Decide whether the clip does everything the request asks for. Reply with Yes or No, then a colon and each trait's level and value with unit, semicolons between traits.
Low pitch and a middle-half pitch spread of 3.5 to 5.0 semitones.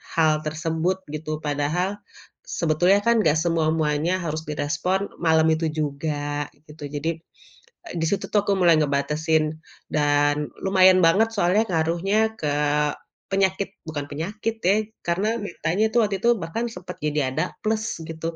No: medium, 165 Hz; average, 4.0 semitones